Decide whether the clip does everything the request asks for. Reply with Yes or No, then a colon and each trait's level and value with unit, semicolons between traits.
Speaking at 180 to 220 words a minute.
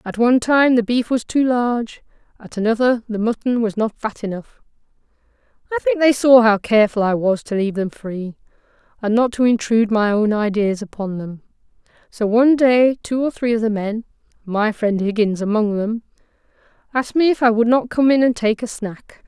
Yes: average, 190 wpm